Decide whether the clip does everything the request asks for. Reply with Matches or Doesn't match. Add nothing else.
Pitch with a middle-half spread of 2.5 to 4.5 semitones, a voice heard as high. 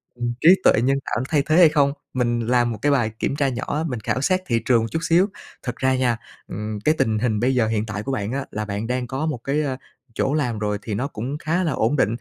Doesn't match